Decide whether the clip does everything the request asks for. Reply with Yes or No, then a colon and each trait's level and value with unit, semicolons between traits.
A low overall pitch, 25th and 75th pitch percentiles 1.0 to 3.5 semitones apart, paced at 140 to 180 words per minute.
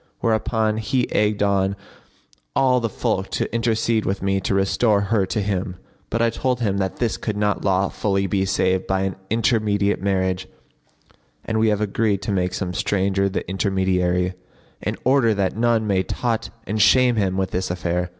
Yes: low, 100 Hz; narrow, 2.6 semitones; average, 175 wpm